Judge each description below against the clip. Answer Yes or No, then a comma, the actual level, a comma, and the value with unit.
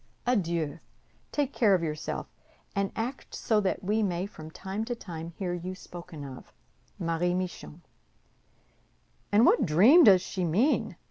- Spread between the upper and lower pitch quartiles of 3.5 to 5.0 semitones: Yes, average, 4.2 semitones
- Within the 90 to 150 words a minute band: Yes, average, 145 wpm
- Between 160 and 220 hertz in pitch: Yes, medium, 185 Hz